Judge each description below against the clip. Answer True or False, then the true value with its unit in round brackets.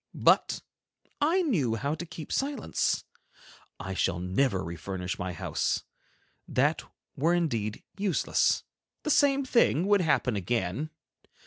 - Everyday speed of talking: False (120 wpm)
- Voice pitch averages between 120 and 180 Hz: True (140 Hz)